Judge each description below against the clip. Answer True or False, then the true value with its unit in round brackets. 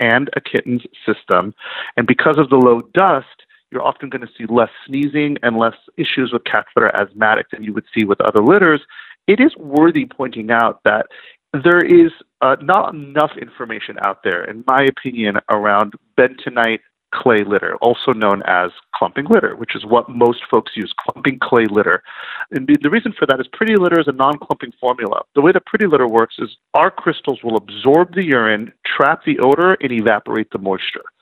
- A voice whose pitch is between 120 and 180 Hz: True (135 Hz)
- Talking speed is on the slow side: False (190 wpm)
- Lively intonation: True (6.4 semitones)